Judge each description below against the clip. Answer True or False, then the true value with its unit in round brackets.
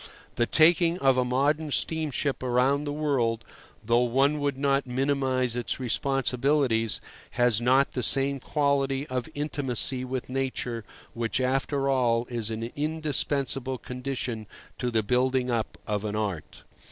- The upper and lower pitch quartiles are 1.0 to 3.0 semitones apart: True (2.6 semitones)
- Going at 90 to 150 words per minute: True (140 wpm)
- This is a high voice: False (130 Hz)